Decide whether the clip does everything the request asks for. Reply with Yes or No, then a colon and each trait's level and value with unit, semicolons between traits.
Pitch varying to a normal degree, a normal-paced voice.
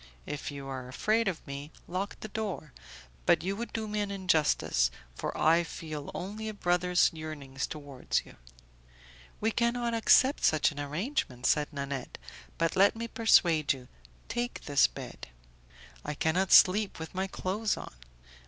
No: wide, 6.5 semitones; average, 155 wpm